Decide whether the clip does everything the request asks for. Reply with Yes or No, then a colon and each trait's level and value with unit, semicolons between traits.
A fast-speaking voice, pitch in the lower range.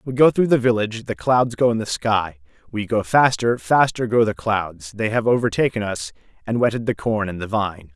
Yes: fast, 220 wpm; low, 110 Hz